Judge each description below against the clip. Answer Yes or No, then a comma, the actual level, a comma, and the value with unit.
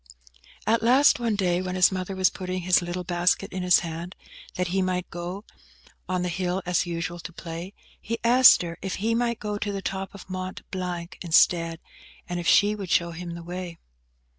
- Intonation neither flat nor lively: No, narrow, 1.9 semitones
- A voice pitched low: No, medium, 180 Hz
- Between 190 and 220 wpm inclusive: Yes, average, 200 wpm